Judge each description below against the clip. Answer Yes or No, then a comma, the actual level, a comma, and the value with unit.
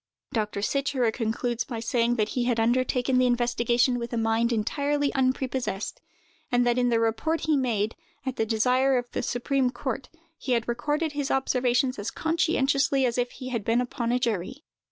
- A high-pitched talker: Yes, high, 245 Hz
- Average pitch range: No, narrow, 2.3 semitones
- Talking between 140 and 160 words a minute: No, average, 180 wpm